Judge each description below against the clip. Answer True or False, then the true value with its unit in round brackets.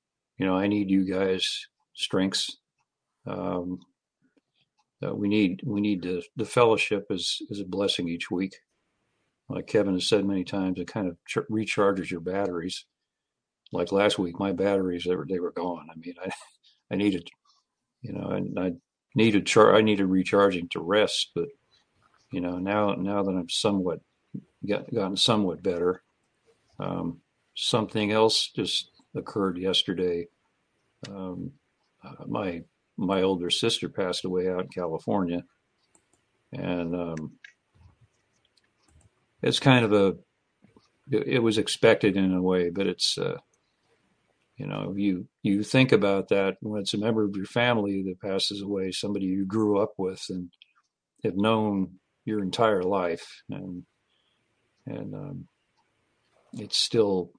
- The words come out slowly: False (145 wpm)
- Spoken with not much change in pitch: True (2.2 semitones)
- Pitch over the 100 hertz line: False (95 Hz)